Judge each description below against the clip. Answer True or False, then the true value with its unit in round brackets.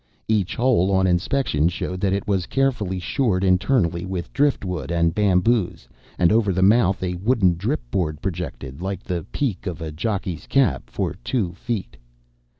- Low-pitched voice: True (95 Hz)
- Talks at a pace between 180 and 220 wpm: False (165 wpm)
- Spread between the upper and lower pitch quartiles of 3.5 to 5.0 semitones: True (3.8 semitones)